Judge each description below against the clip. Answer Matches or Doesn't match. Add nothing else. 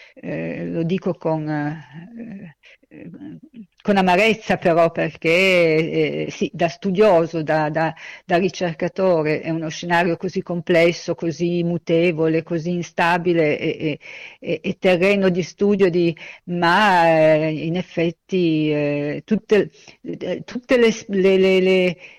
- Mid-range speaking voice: Matches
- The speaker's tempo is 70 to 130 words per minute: Matches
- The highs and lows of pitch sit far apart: Doesn't match